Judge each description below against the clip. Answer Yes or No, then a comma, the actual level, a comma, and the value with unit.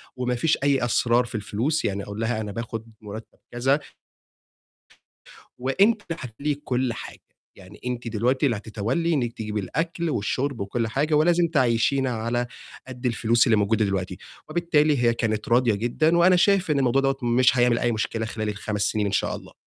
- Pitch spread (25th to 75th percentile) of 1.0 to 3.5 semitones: No, average, 4.1 semitones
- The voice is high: No, low, 120 Hz